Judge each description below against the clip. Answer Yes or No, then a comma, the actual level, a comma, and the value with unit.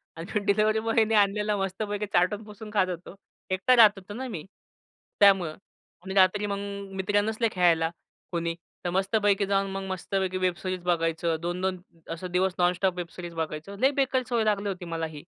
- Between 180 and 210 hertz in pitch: Yes, high, 190 Hz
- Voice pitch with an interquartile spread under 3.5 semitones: Yes, average, 2.8 semitones